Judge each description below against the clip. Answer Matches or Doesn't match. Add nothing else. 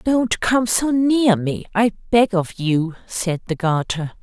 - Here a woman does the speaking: Matches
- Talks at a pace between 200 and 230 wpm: Doesn't match